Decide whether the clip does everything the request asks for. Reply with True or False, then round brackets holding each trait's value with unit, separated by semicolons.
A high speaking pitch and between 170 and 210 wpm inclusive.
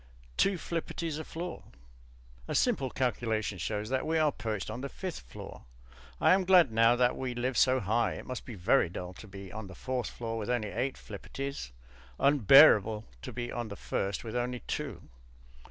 False (120 Hz; 185 wpm)